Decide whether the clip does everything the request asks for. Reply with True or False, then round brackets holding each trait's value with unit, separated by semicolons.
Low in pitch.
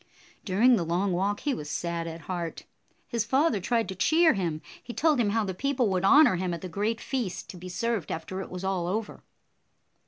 False (195 Hz)